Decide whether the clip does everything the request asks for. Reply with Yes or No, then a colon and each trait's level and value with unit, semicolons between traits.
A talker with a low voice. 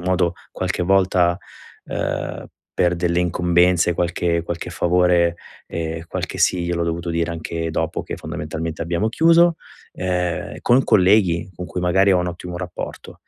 Yes: very low, 90 Hz